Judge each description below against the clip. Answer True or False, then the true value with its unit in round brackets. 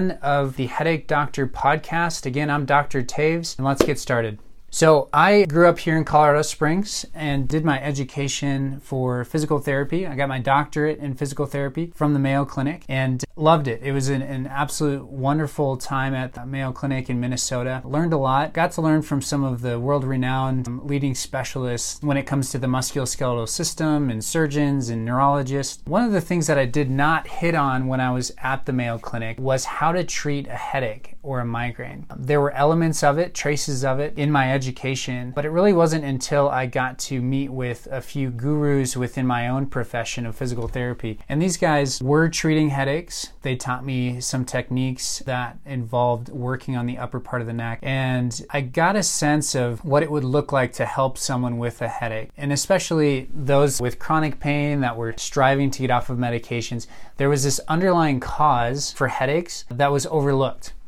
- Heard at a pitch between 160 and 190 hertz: False (140 Hz)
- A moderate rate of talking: True (195 wpm)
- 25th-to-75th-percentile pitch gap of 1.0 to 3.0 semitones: True (2.6 semitones)